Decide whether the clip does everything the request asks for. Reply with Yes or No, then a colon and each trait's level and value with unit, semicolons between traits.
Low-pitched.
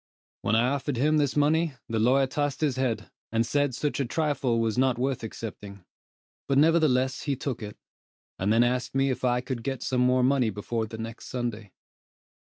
Yes: low, 125 Hz